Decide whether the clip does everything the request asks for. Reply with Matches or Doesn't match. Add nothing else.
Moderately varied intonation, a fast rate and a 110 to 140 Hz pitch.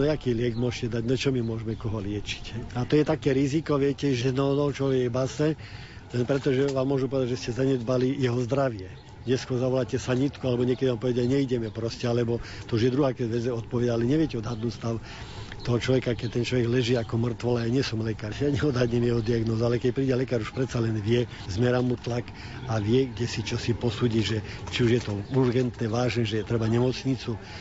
Doesn't match